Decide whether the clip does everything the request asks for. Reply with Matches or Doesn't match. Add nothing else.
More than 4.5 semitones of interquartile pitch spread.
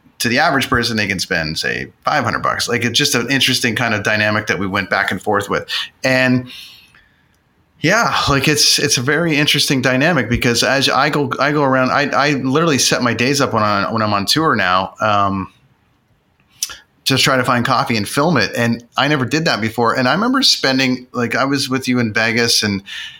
Doesn't match